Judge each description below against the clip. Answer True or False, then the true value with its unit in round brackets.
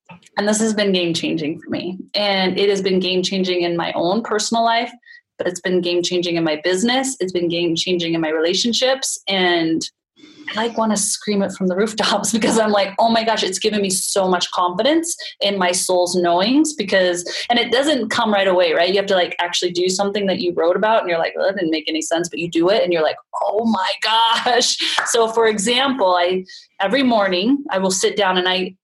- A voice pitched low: False (195 Hz)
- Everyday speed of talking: False (230 wpm)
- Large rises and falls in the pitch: False (4.2 semitones)